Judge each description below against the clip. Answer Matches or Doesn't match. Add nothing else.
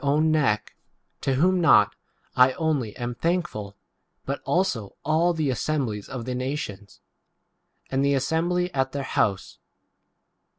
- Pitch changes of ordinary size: Matches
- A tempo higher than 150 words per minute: Doesn't match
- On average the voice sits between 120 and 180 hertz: Matches